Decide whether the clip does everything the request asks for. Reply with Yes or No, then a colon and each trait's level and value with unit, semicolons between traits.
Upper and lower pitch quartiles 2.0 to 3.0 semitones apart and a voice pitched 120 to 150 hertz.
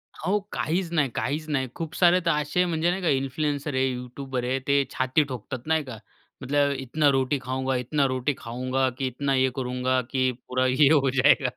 Yes: average, 2.7 semitones; low, 135 Hz